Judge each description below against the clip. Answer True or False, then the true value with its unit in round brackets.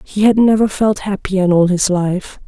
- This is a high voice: True (195 Hz)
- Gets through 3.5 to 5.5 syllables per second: True (4.7 syllables/s)